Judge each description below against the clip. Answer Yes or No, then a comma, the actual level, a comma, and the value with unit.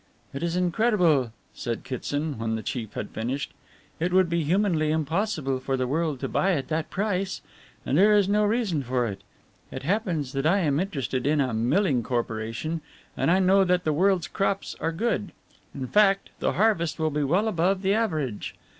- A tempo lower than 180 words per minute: No, average, 190 wpm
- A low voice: No, medium, 160 Hz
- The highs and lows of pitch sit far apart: Yes, wide, 6.2 semitones